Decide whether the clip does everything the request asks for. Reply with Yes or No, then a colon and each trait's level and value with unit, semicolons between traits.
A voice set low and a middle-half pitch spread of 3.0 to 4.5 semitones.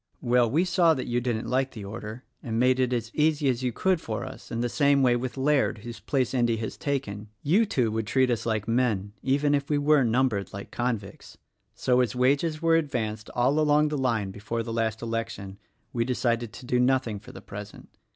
Yes: low, 125 Hz; average, 3.6 semitones